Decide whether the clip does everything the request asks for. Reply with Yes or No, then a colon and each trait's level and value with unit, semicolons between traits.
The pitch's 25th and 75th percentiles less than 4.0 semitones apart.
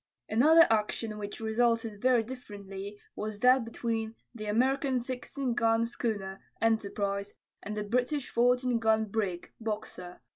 Yes: average, 2.8 semitones